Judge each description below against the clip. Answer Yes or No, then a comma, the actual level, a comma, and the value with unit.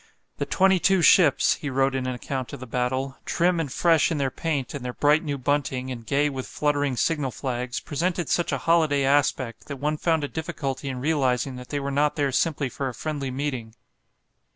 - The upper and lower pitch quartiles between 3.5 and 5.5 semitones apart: No, average, 2.8 semitones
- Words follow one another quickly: Yes, fast, 210 wpm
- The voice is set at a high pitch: No, medium, 140 Hz